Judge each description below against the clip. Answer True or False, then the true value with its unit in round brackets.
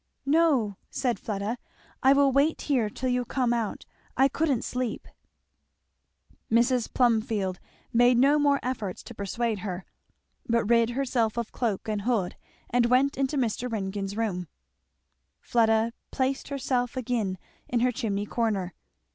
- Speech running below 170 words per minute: True (140 wpm)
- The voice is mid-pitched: False (235 Hz)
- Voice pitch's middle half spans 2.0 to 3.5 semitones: True (3.2 semitones)